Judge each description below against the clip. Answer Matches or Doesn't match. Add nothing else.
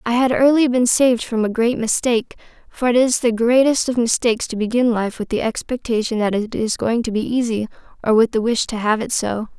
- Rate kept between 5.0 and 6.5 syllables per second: Matches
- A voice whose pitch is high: Matches